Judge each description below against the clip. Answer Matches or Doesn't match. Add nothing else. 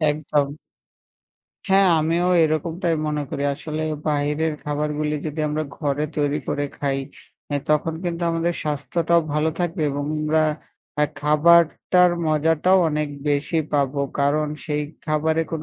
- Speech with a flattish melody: Matches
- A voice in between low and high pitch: Matches